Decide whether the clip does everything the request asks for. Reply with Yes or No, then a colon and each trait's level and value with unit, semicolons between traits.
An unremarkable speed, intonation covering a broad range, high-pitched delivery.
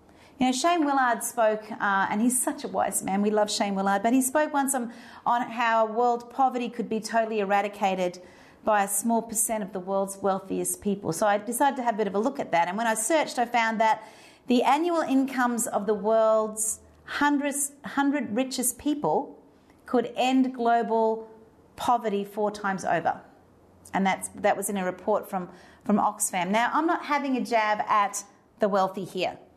No: average, 190 wpm; average, 3.6 semitones; high, 225 Hz